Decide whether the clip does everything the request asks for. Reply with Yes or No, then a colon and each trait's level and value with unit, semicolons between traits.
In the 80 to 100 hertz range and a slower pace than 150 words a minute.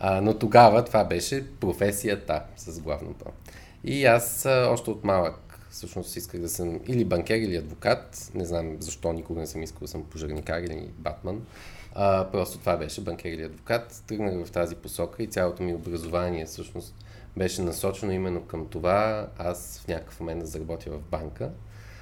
No: very low, 90 Hz; fast, 165 wpm